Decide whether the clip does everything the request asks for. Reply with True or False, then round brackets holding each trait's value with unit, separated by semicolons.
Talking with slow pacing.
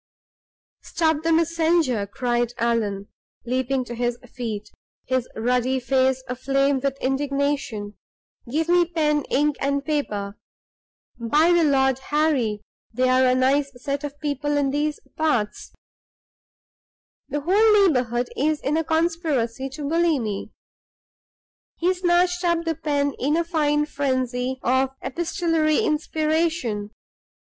True (120 wpm)